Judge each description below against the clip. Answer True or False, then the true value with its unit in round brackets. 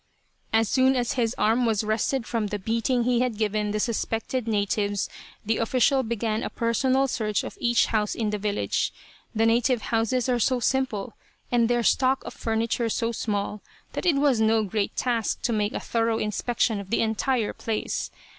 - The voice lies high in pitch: True (225 Hz)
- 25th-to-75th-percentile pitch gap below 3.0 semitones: True (2.4 semitones)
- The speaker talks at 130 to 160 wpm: False (185 wpm)